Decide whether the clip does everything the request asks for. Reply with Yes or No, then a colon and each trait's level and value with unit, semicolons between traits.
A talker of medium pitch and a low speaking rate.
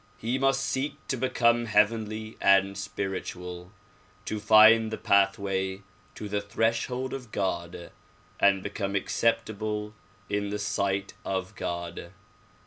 No: low, 105 Hz; slow, 125 wpm